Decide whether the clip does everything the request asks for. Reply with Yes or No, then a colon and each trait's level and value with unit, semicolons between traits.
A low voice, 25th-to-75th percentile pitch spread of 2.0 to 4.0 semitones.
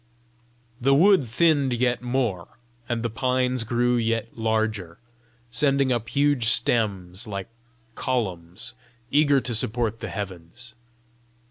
Yes: low, 120 Hz; average, 2.8 semitones